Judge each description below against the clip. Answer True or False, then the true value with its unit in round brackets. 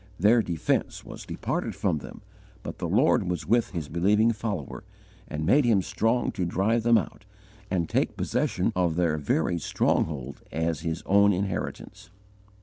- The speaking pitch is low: True (90 Hz)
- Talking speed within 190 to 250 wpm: False (155 wpm)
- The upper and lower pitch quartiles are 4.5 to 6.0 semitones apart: True (4.9 semitones)